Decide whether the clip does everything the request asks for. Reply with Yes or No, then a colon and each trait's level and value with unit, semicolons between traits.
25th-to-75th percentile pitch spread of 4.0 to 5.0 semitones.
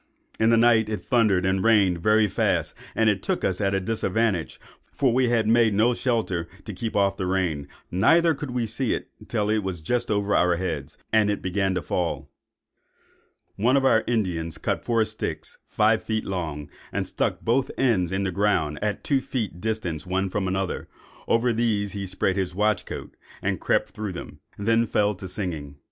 No: average, 3.5 semitones